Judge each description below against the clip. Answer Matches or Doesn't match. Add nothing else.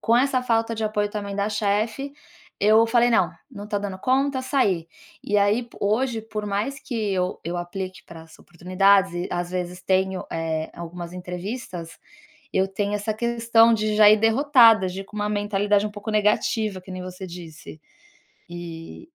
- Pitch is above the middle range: Matches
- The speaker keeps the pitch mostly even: Doesn't match